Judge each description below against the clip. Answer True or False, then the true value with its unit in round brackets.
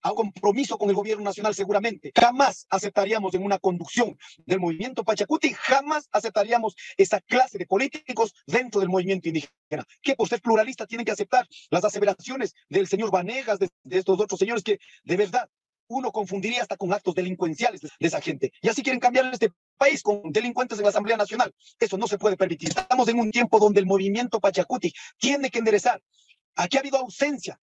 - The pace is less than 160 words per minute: False (190 wpm)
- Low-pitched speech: False (215 Hz)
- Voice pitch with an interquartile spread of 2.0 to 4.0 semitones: False (4.4 semitones)